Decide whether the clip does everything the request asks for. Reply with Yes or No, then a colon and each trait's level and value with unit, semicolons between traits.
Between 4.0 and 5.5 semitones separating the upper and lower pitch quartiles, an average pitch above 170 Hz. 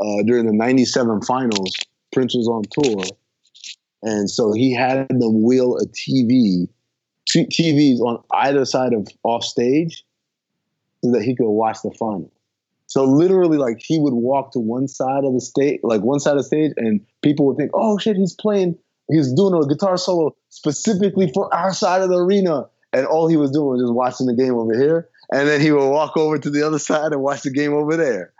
No: average, 4.8 semitones; medium, 140 Hz